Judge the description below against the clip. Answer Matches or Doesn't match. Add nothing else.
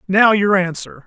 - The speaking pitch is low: Doesn't match